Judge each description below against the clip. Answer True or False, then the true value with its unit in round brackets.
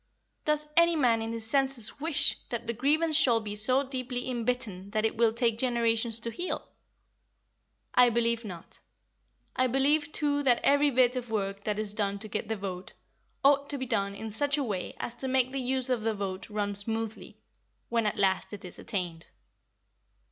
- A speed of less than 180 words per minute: False (190 wpm)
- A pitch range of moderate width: True (3.9 semitones)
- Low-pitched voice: False (235 Hz)